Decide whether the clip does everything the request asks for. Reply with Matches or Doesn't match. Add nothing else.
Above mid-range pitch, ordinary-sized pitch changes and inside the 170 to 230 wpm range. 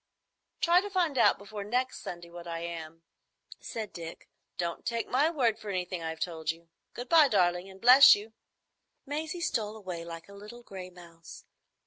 Doesn't match